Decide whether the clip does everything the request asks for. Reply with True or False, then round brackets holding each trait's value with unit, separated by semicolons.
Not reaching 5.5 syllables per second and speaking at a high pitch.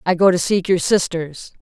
False (4.9 syllables/s; 180 Hz)